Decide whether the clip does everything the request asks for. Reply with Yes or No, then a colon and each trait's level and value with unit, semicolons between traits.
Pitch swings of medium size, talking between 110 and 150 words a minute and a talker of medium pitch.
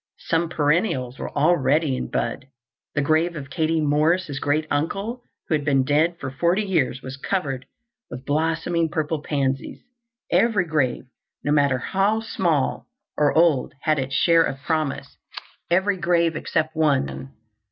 Yes: average, 3.7 semitones; average, 140 wpm; medium, 155 Hz